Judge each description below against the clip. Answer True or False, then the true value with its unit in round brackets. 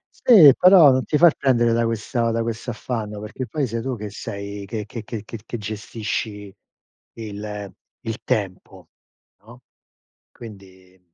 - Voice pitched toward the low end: True (110 Hz)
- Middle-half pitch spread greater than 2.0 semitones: True (2.7 semitones)